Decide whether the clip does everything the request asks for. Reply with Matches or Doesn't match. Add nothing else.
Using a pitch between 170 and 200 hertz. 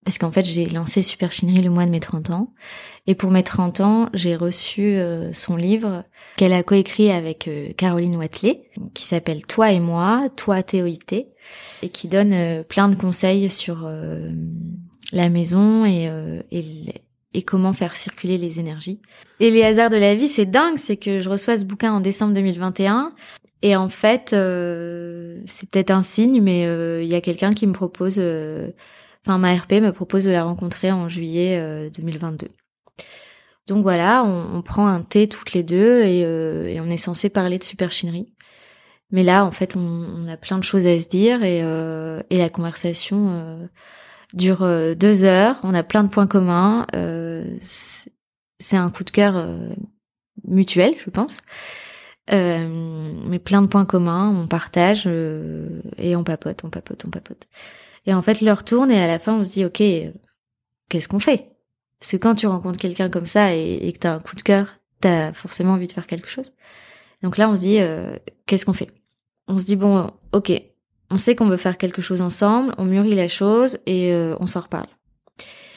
Matches